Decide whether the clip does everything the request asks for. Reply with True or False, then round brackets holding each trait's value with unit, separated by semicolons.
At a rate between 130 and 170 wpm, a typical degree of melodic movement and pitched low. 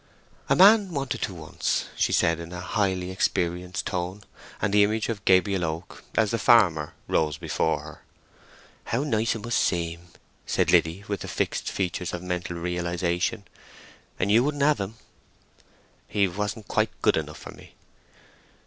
True (160 wpm; 4.0 semitones; 95 Hz)